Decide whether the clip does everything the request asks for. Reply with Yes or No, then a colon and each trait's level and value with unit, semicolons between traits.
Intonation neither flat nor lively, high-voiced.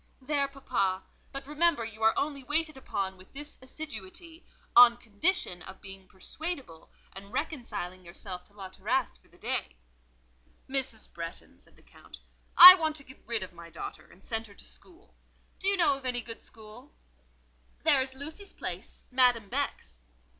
No: wide, 7.2 semitones; high, 245 Hz